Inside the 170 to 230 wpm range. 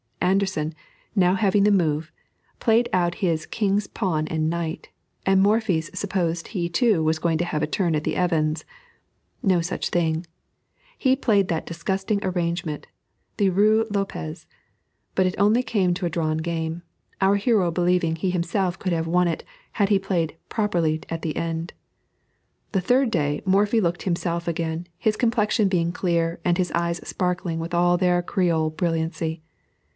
No: average, 160 wpm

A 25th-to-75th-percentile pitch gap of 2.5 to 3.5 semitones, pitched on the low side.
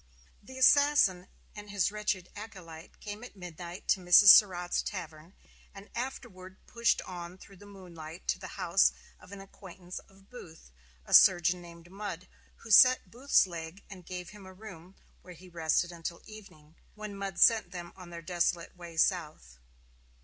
No: average, 3.0 semitones; medium, 185 Hz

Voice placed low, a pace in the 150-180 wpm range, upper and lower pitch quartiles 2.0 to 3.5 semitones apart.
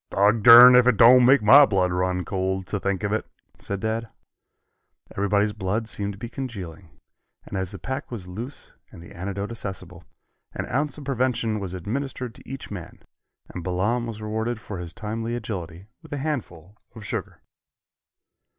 No: low, 105 Hz; average, 170 wpm; average, 4.2 semitones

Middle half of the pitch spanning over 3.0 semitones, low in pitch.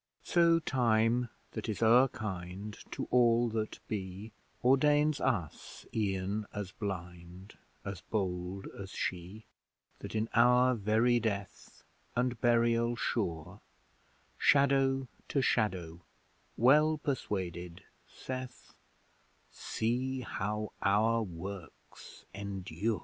Yes: average, 4.3 semitones; low, 110 Hz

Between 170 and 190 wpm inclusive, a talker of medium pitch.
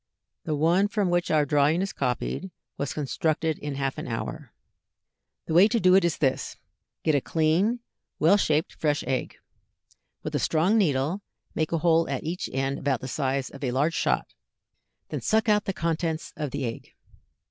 Yes: average, 180 wpm; medium, 155 Hz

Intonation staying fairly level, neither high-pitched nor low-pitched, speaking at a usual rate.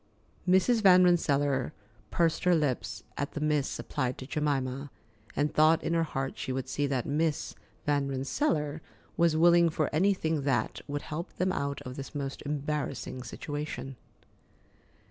No: average, 3.2 semitones; medium, 145 Hz; average, 150 wpm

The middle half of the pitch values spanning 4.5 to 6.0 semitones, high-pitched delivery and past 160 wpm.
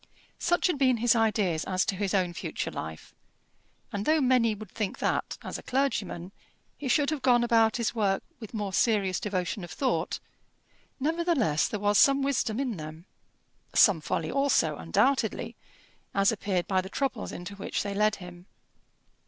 Yes: wide, 5.5 semitones; high, 210 Hz; average, 170 wpm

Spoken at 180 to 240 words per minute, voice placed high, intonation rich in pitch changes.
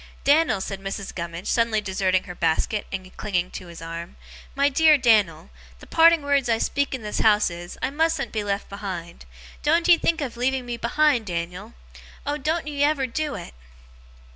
Yes: average, 185 wpm; high, 225 Hz; wide, 7.4 semitones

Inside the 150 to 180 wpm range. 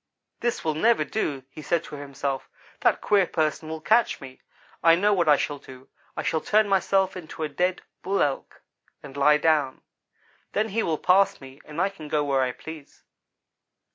No: average, 190 wpm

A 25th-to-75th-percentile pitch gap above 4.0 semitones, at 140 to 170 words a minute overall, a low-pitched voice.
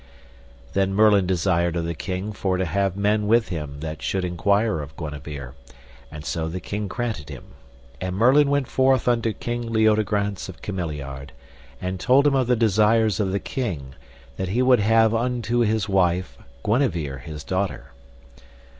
Yes: average, 4.7 semitones; average, 165 wpm; low, 100 Hz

